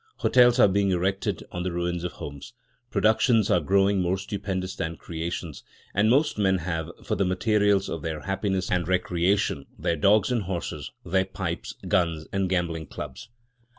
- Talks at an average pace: Yes, average, 165 wpm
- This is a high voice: No, very low, 95 Hz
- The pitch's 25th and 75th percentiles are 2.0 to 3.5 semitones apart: Yes, average, 2.7 semitones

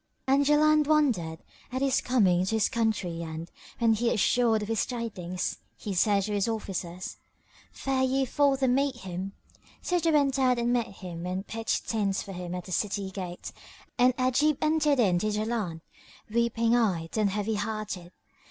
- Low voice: No, high, 220 Hz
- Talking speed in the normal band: Yes, average, 170 wpm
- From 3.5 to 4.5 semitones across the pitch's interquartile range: No, average, 5.3 semitones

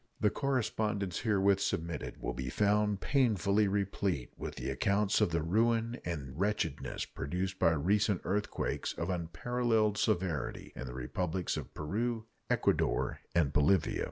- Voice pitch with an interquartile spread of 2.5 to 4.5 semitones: Yes, average, 4.1 semitones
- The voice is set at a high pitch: No, low, 100 Hz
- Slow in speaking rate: Yes, slow, 130 wpm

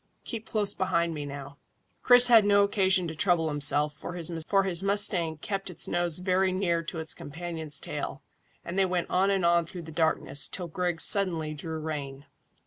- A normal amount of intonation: Yes, average, 3.3 semitones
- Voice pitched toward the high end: No, medium, 170 Hz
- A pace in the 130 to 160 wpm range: No, average, 180 wpm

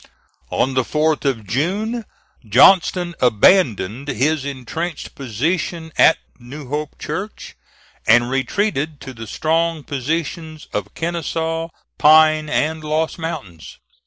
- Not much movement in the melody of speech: No, average, 4.0 semitones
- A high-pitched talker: No, medium, 155 Hz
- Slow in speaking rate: Yes, slow, 110 wpm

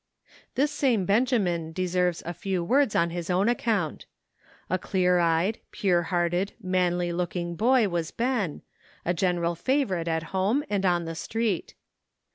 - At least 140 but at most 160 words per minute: Yes, average, 145 wpm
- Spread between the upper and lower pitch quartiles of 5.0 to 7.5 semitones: No, average, 3.6 semitones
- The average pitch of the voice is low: No, medium, 180 Hz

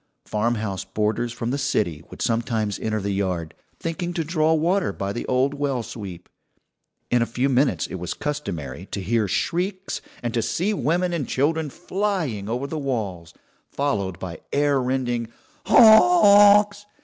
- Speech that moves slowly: No, average, 155 wpm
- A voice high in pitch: No, low, 130 Hz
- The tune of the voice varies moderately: No, wide, 7.4 semitones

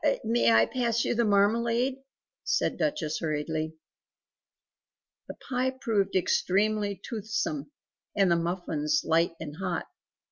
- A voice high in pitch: Yes, high, 200 Hz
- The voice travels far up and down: Yes, wide, 6.2 semitones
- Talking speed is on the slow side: Yes, slow, 115 wpm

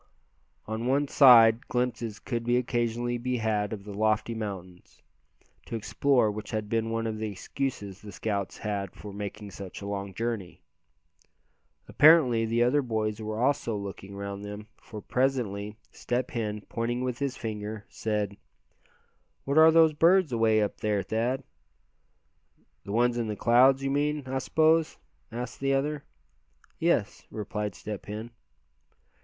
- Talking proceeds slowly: No, average, 150 wpm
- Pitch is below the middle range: Yes, low, 115 Hz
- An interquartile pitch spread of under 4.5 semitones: Yes, average, 3.3 semitones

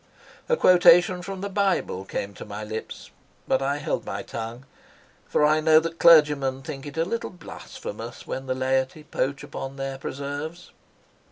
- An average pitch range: Yes, average, 4.3 semitones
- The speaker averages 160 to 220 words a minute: Yes, average, 165 wpm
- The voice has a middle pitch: Yes, medium, 145 Hz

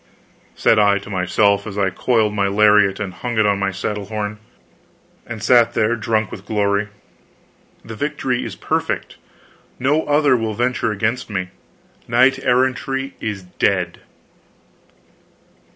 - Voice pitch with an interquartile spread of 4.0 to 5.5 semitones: No, average, 3.4 semitones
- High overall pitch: No, low, 105 Hz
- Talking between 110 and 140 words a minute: Yes, slow, 135 wpm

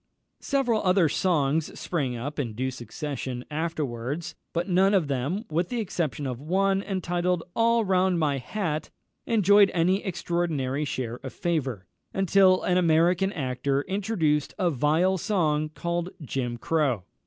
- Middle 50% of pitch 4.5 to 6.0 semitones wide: Yes, average, 5.1 semitones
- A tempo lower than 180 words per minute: Yes, average, 140 wpm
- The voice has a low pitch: No, medium, 165 Hz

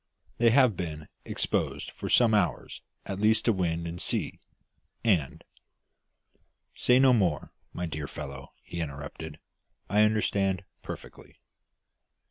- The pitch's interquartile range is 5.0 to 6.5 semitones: Yes, wide, 5.5 semitones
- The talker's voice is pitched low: Yes, very low, 95 Hz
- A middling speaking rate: No, slow, 125 wpm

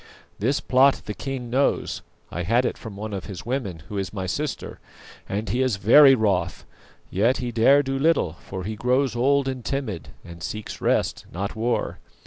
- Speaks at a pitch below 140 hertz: Yes, low, 115 Hz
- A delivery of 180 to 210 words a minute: Yes, average, 185 wpm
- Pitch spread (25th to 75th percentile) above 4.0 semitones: Yes, average, 5.1 semitones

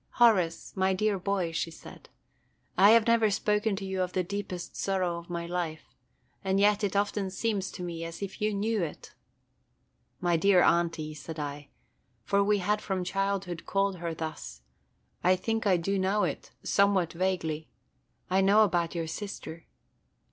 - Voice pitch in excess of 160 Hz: Yes, high, 190 Hz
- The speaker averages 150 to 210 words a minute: Yes, average, 170 wpm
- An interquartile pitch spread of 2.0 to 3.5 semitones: Yes, average, 2.9 semitones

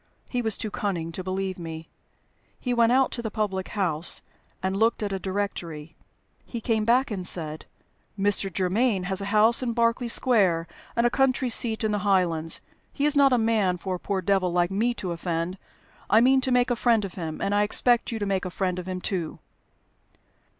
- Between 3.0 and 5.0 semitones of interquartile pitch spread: Yes, average, 4.3 semitones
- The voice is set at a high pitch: Yes, high, 200 Hz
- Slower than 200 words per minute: No, fast, 205 wpm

